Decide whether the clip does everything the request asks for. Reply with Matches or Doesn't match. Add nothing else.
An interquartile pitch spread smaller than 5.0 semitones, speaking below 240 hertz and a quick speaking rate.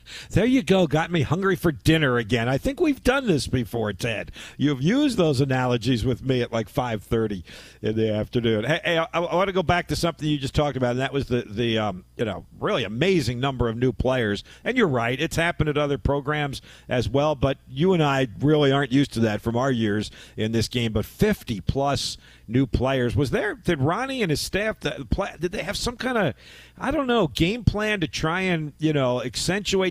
Doesn't match